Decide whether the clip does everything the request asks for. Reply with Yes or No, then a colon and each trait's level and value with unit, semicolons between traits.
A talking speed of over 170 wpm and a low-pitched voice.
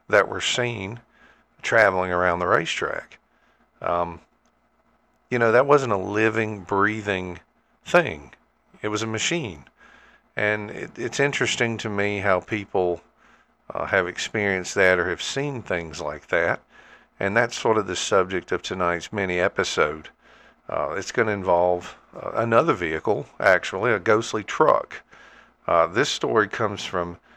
No: average, 145 wpm; low, 100 Hz